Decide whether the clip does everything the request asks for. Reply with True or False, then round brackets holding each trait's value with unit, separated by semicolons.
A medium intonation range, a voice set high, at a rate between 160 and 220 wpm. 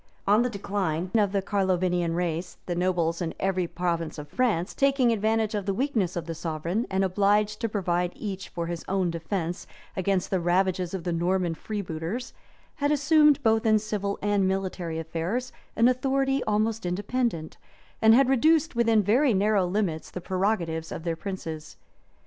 True (4.2 semitones; 195 Hz; 165 wpm)